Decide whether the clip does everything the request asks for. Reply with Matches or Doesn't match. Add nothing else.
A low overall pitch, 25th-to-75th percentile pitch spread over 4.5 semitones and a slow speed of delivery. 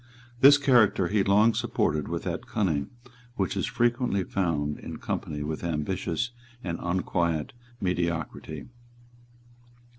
Matches